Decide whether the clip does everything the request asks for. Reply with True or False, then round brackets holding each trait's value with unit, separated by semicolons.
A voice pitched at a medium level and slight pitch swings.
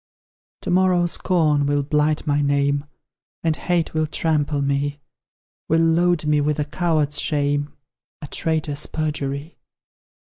True (150 Hz; 2.1 semitones)